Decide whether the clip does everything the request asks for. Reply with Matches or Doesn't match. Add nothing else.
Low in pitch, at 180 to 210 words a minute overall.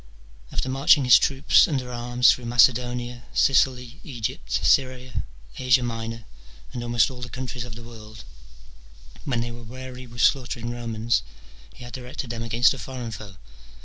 Doesn't match